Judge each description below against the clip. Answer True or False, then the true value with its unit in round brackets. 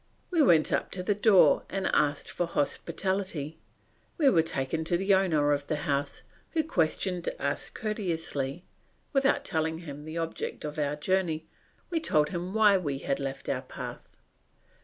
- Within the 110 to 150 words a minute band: False (160 wpm)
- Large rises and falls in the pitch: False (4.5 semitones)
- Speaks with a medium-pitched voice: True (165 Hz)